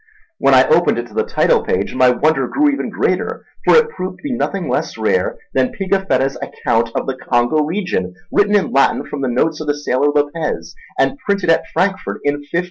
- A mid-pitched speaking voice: Yes, medium, 165 Hz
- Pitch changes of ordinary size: No, wide, 7.1 semitones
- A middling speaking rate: No, fast, 210 wpm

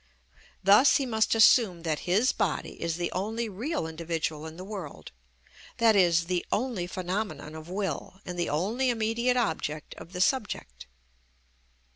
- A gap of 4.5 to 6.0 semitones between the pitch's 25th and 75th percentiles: Yes, average, 5.1 semitones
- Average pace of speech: Yes, average, 145 wpm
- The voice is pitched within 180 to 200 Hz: Yes, medium, 185 Hz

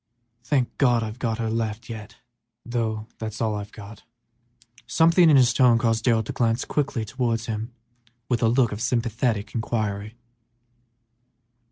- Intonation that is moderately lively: No, narrow, 2.0 semitones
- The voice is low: Yes, low, 115 Hz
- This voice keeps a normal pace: Yes, average, 150 wpm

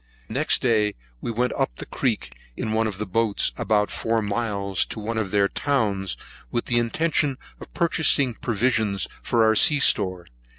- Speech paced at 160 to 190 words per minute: Yes, average, 170 wpm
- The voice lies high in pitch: No, low, 110 Hz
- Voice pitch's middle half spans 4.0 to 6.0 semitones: No, average, 2.8 semitones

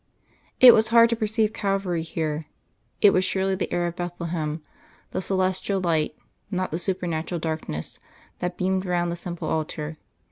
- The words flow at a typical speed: Yes, average, 155 wpm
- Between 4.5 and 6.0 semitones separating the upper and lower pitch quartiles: No, average, 2.9 semitones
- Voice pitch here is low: No, medium, 180 Hz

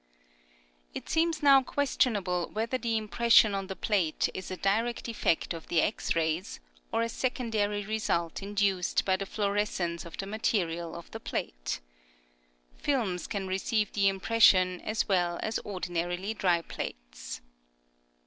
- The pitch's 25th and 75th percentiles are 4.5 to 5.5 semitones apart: No, average, 4.0 semitones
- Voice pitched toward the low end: No, high, 195 Hz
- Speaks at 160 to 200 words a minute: No, average, 140 wpm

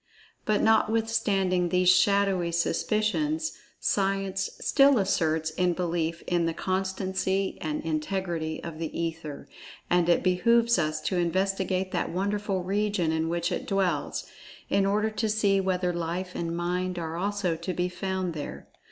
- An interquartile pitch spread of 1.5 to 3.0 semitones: Yes, average, 2.7 semitones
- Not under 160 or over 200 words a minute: No, average, 145 wpm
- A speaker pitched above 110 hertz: Yes, medium, 185 Hz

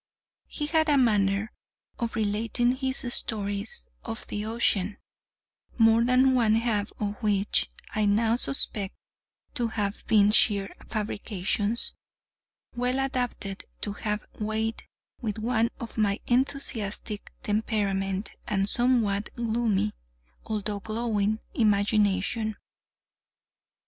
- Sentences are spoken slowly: Yes, slow, 105 wpm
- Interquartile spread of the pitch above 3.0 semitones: No, narrow, 2.6 semitones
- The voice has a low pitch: No, high, 220 Hz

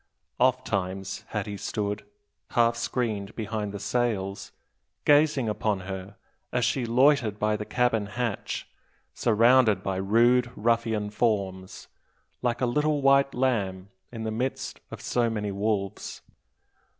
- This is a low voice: Yes, low, 110 Hz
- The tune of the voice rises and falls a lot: No, average, 3.3 semitones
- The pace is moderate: No, slow, 125 wpm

